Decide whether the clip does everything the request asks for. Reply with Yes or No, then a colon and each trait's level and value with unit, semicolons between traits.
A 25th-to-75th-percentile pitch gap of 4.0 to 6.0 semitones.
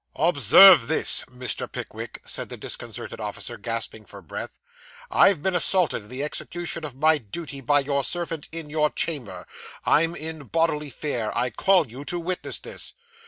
Yes: average, 4.9 semitones